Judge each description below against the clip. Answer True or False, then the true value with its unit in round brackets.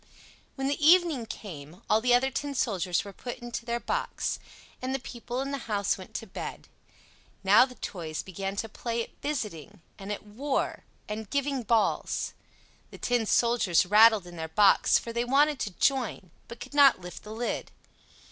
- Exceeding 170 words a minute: True (180 wpm)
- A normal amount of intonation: True (4.8 semitones)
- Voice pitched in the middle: False (230 Hz)